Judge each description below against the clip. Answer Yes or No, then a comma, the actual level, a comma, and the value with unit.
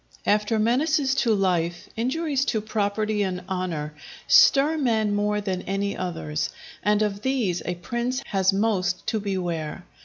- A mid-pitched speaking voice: No, high, 205 Hz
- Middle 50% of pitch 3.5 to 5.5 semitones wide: Yes, average, 4.0 semitones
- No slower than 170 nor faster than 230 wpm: No, average, 145 wpm